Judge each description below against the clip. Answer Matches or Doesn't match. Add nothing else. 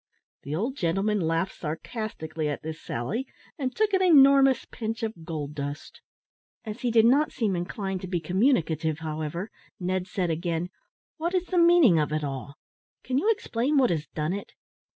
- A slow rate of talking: Doesn't match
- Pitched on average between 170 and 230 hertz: Matches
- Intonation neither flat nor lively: Doesn't match